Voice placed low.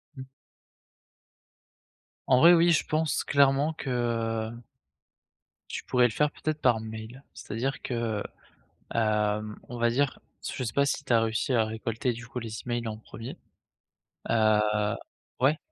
Yes: low, 120 Hz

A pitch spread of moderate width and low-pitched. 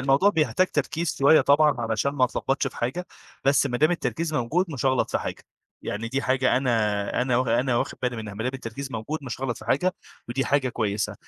Yes: average, 3.3 semitones; low, 130 Hz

